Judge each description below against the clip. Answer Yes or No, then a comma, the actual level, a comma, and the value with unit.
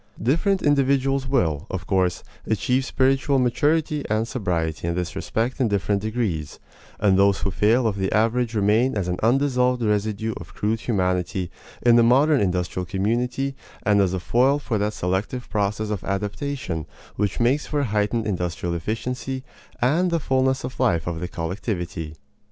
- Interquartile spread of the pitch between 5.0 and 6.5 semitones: Yes, average, 5.3 semitones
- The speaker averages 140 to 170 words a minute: Yes, average, 165 wpm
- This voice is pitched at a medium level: No, low, 110 Hz